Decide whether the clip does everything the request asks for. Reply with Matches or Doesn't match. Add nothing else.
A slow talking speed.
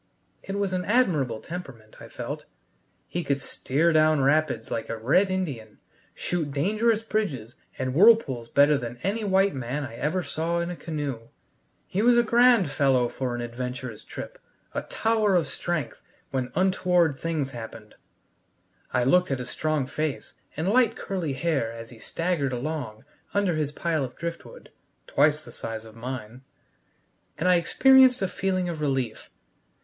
Doesn't match